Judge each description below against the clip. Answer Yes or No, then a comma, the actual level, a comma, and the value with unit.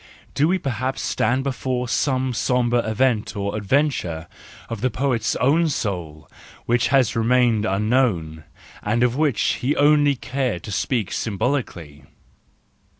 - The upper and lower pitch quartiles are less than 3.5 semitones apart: No, average, 4.2 semitones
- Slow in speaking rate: Yes, slow, 130 wpm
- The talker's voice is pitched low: Yes, low, 120 Hz